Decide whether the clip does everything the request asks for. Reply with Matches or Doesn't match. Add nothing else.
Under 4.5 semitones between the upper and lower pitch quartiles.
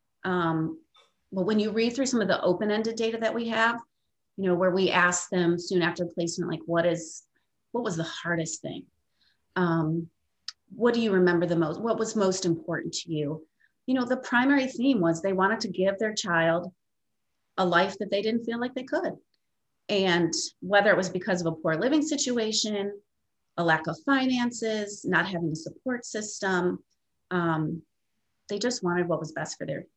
Doesn't match